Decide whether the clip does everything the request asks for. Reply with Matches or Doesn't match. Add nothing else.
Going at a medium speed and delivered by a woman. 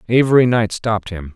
Doesn't match